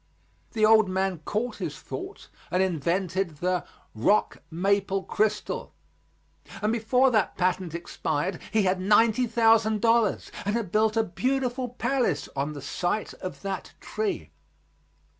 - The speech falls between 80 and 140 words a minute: Yes, slow, 135 wpm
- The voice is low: No, high, 205 Hz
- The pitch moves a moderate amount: Yes, average, 3.7 semitones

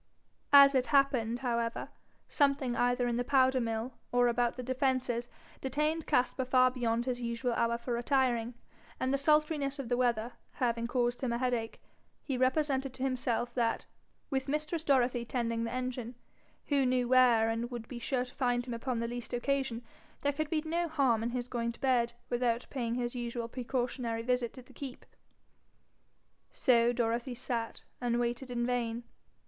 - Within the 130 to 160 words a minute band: No, average, 175 wpm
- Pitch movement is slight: Yes, narrow, 1.9 semitones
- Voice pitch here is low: No, high, 245 Hz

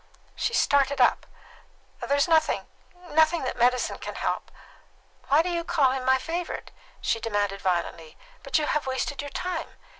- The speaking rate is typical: Yes, average, 160 wpm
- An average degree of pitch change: Yes, average, 4.2 semitones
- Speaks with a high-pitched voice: Yes, very high, 280 Hz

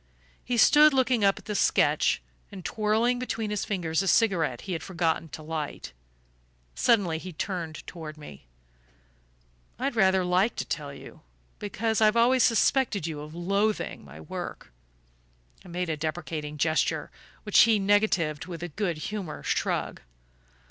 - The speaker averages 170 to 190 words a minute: No, average, 150 wpm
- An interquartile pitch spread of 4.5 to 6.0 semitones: Yes, average, 5.2 semitones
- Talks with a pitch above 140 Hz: Yes, medium, 185 Hz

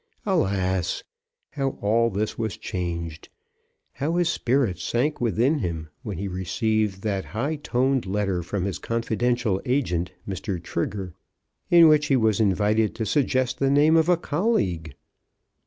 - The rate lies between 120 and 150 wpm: Yes, average, 140 wpm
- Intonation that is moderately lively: No, wide, 6.2 semitones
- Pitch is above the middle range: No, low, 110 Hz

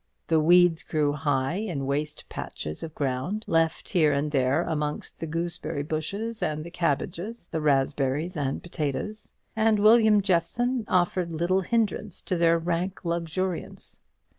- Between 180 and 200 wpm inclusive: No, average, 140 wpm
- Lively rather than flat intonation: No, average, 3.9 semitones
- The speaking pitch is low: No, medium, 165 Hz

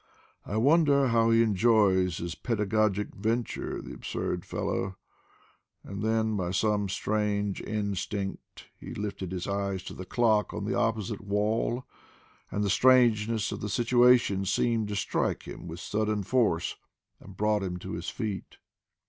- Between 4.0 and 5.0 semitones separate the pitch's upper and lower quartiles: No, narrow, 2.5 semitones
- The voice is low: Yes, low, 105 Hz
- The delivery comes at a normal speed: Yes, average, 150 wpm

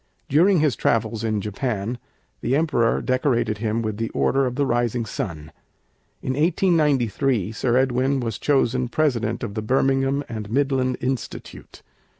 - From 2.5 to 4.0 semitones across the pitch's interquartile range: Yes, average, 3.4 semitones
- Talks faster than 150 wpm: No, average, 145 wpm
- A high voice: No, low, 125 Hz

